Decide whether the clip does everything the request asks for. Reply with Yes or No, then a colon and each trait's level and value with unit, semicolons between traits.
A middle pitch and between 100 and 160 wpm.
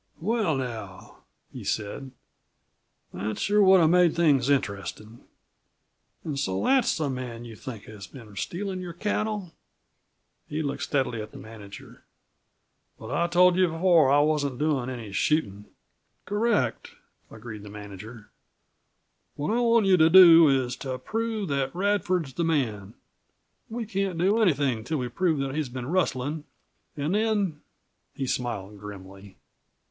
Yes: medium, 145 Hz; average, 150 wpm